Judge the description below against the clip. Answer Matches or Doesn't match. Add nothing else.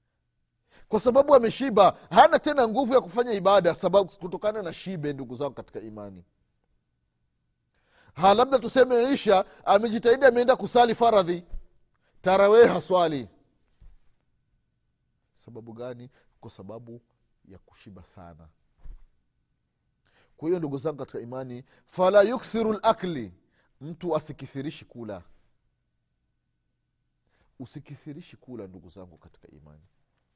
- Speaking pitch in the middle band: Matches